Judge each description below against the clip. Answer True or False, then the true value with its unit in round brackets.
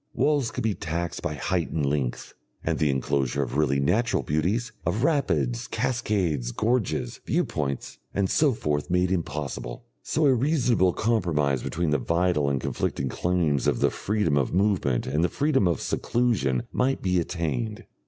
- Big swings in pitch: True (7.7 semitones)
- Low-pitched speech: True (85 Hz)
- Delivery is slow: False (160 wpm)